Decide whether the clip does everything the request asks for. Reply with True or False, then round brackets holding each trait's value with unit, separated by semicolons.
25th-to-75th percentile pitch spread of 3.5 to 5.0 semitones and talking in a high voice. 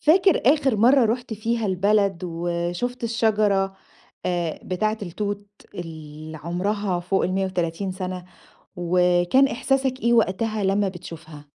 True (4.0 semitones; 195 Hz)